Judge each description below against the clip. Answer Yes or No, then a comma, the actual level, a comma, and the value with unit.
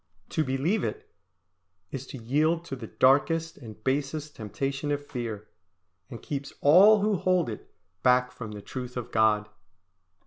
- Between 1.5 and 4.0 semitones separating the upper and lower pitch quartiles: No, average, 4.9 semitones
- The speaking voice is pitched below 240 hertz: Yes, low, 135 Hz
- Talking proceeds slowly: No, average, 150 wpm